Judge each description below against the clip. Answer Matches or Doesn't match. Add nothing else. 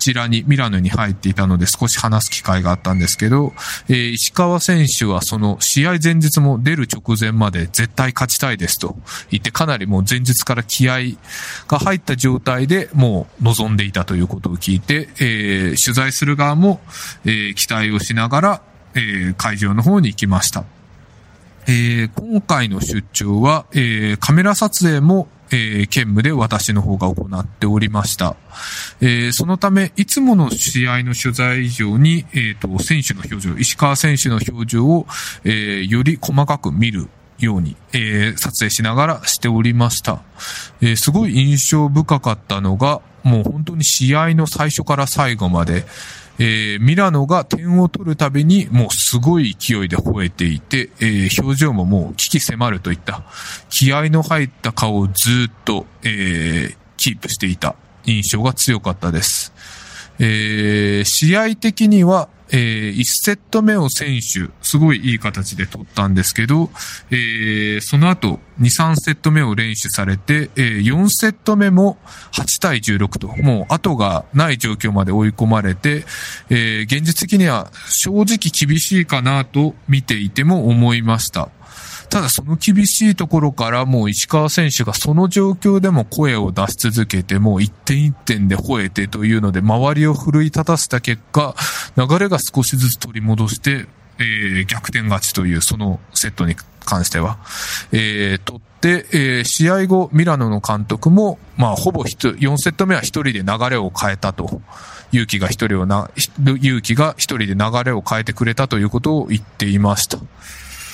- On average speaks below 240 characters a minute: Doesn't match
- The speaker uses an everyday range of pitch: Doesn't match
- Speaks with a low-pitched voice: Matches